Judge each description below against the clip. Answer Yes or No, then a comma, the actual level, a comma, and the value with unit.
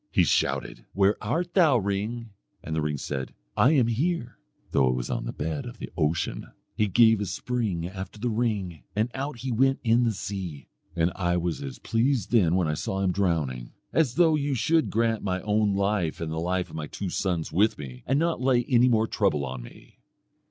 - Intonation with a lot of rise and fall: Yes, wide, 6.2 semitones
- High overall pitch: No, low, 100 Hz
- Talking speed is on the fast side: Yes, fast, 210 wpm